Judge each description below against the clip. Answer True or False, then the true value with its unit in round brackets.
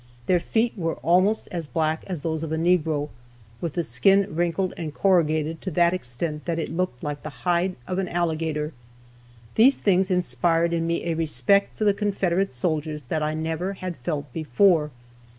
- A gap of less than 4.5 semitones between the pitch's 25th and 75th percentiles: True (2.9 semitones)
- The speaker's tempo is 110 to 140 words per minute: False (180 wpm)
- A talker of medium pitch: True (165 Hz)